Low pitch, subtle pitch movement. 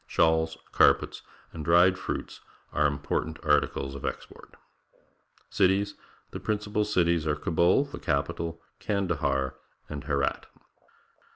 No: very low, 80 Hz; average, 4.3 semitones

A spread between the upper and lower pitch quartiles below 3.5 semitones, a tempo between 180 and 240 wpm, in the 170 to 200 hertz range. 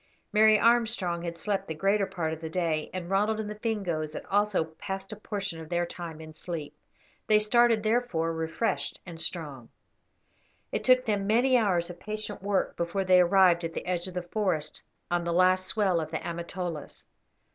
No: average, 3.9 semitones; average, 190 wpm; medium, 185 Hz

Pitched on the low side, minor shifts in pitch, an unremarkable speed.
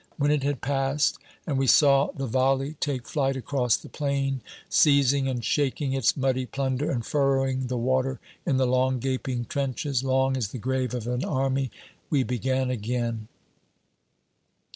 Yes: low, 130 Hz; narrow, 1.4 semitones; average, 160 wpm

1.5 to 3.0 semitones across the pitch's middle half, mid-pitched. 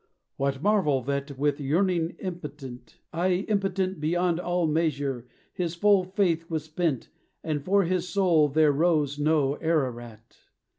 No: average, 4.2 semitones; medium, 160 Hz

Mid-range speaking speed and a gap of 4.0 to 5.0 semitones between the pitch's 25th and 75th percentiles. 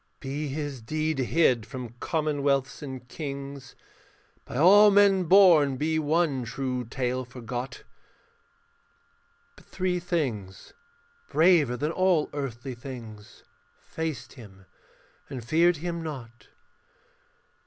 No: slow, 105 wpm; average, 4.5 semitones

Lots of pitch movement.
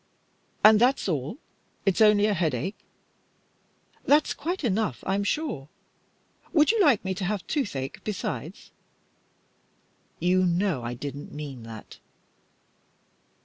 Yes: wide, 7.2 semitones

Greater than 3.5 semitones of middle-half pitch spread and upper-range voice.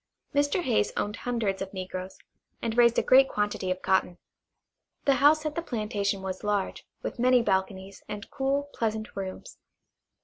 Yes: average, 5.0 semitones; high, 210 Hz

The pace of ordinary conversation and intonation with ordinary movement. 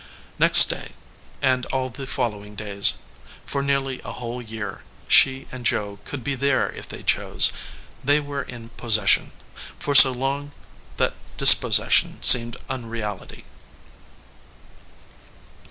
No: slow, 120 wpm; average, 3.4 semitones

